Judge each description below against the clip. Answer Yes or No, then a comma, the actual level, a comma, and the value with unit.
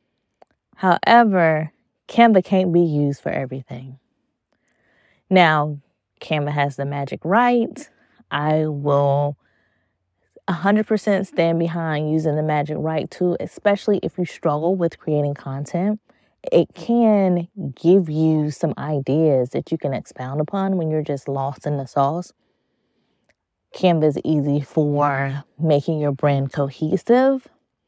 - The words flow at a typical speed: No, slow, 120 wpm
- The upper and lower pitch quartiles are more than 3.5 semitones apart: Yes, average, 4.2 semitones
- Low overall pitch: No, medium, 155 Hz